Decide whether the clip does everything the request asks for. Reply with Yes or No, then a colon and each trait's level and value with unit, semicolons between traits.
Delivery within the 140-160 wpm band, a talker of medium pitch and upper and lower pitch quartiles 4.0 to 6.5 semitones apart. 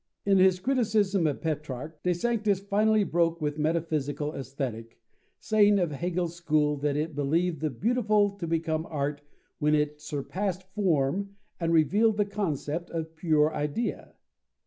Yes: average, 145 wpm; medium, 165 Hz; average, 4.9 semitones